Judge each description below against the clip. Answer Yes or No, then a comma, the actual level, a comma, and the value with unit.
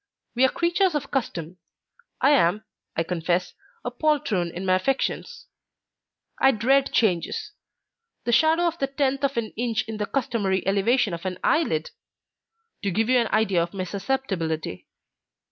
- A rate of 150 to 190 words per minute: Yes, average, 155 wpm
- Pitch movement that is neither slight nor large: No, wide, 6.6 semitones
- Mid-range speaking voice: No, high, 225 Hz